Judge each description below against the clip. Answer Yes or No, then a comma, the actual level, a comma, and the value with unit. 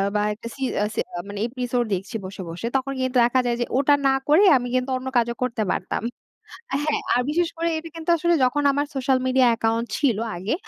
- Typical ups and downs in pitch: Yes, average, 3.5 semitones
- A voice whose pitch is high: Yes, very high, 255 Hz